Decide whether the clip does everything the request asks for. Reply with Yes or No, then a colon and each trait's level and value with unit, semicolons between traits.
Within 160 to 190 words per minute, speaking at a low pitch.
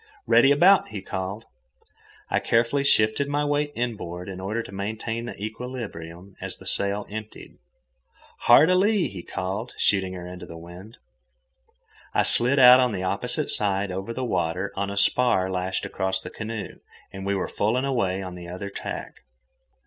Yes: average, 170 wpm; low, 100 Hz